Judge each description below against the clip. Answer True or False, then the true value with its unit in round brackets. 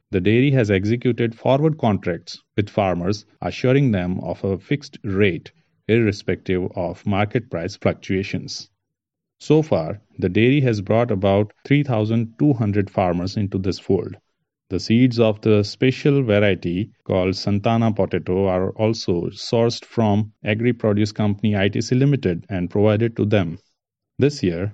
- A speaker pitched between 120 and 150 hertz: False (105 Hz)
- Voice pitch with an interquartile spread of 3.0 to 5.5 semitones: True (3.6 semitones)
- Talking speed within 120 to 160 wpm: True (135 wpm)